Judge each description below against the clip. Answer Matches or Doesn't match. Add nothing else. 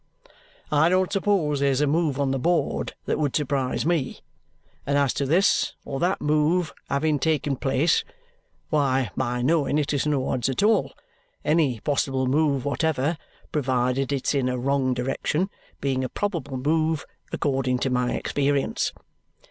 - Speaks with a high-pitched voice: Doesn't match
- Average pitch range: Matches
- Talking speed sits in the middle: Matches